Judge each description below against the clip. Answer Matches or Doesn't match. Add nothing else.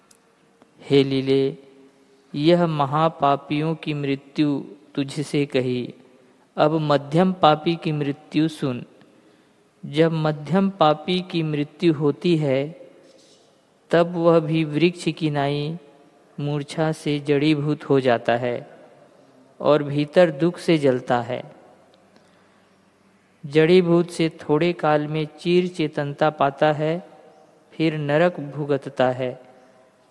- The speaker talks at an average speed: Doesn't match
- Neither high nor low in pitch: Matches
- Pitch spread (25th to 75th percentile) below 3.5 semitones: Matches